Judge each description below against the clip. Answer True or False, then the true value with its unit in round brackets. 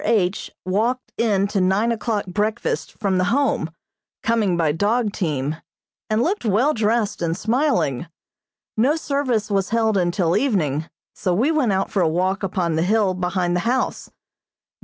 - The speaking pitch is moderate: False (200 Hz)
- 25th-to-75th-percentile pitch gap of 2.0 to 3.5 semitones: False (4.4 semitones)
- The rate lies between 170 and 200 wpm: False (160 wpm)